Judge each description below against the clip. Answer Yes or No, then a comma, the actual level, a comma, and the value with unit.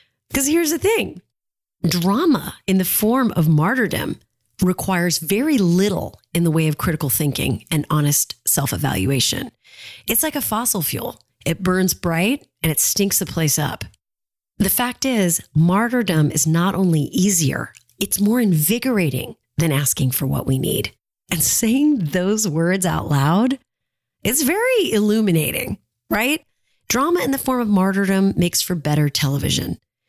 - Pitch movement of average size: No, wide, 6.0 semitones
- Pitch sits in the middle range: Yes, medium, 180 Hz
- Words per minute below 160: Yes, average, 150 wpm